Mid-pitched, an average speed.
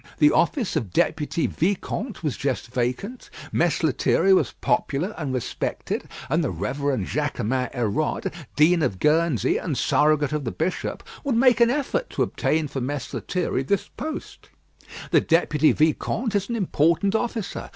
Yes: medium, 155 Hz; average, 150 wpm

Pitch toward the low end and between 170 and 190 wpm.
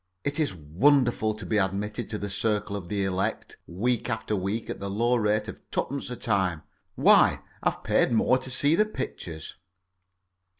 Yes: low, 105 Hz; average, 175 wpm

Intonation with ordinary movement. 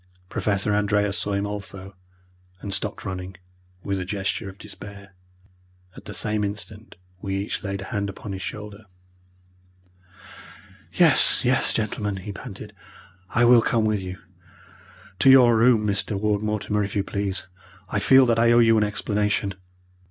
No: narrow, 1.6 semitones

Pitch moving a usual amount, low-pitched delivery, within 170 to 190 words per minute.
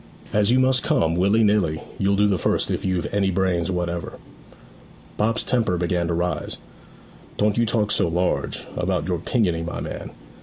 Yes: average, 3.4 semitones; very low, 95 Hz; average, 175 wpm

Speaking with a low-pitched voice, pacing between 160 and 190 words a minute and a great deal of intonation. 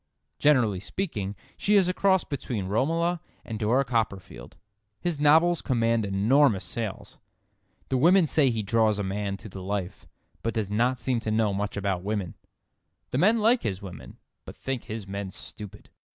Yes: low, 115 Hz; average, 165 wpm; wide, 6.4 semitones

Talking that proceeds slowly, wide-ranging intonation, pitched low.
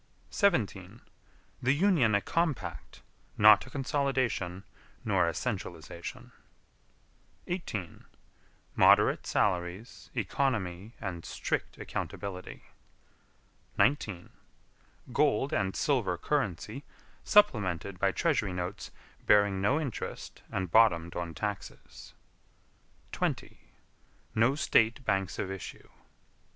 Yes: slow, 90 wpm; wide, 6.5 semitones; low, 105 Hz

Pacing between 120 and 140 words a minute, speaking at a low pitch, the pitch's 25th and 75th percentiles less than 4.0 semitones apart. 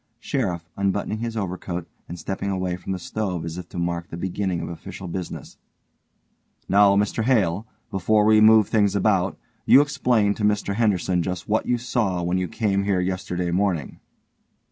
No: average, 170 wpm; very low, 95 Hz; average, 3.1 semitones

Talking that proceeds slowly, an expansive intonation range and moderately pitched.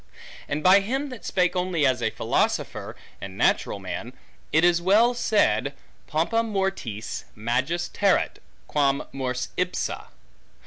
Yes: slow, 130 wpm; wide, 7.6 semitones; medium, 175 Hz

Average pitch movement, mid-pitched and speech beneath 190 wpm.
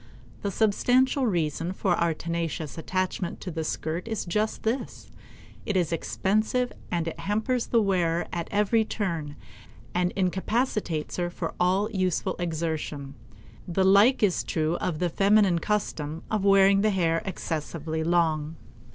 Yes: average, 3.9 semitones; medium, 180 Hz; average, 140 wpm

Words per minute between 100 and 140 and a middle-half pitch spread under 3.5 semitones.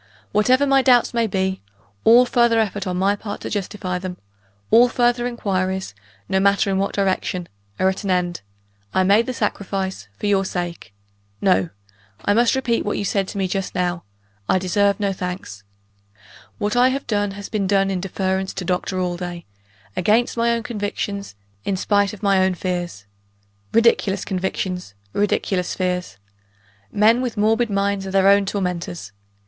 No: average, 165 wpm; narrow, 2.5 semitones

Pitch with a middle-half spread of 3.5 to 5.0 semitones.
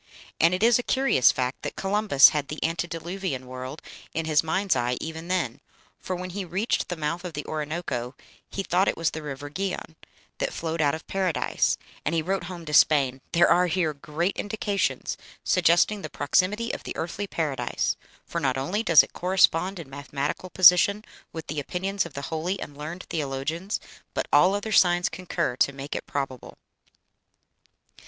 Yes: average, 4.2 semitones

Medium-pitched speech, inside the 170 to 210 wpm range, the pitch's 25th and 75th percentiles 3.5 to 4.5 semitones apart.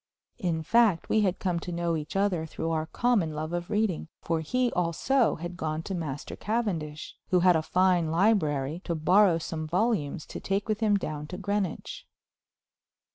Yes: medium, 175 Hz; average, 180 wpm; average, 4.2 semitones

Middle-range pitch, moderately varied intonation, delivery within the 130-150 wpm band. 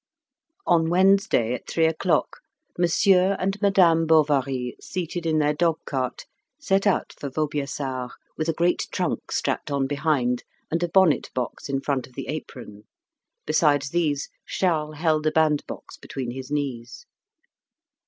Yes: medium, 155 Hz; average, 3.9 semitones; average, 145 wpm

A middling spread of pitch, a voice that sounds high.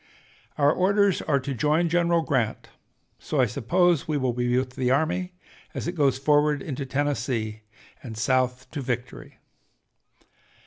No: average, 4.0 semitones; medium, 140 Hz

